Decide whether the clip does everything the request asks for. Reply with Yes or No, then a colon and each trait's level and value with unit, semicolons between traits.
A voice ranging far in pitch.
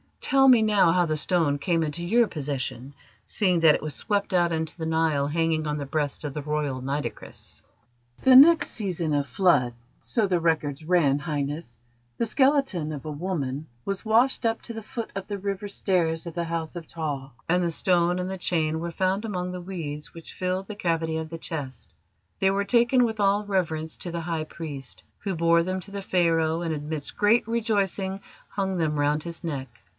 No: average, 4.1 semitones